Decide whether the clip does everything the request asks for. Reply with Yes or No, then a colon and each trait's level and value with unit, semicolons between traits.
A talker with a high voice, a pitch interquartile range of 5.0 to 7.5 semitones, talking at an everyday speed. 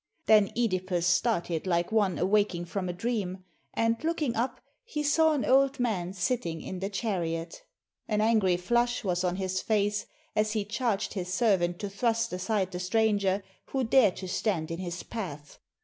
No: high, 200 Hz; average, 4.1 semitones; average, 170 wpm